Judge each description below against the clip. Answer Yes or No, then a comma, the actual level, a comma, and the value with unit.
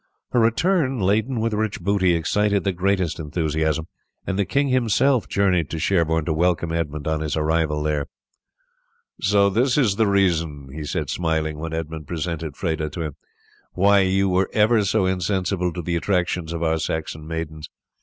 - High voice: No, very low, 90 Hz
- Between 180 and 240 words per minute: No, average, 170 wpm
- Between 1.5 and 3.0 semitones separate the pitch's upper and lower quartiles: No, average, 4.0 semitones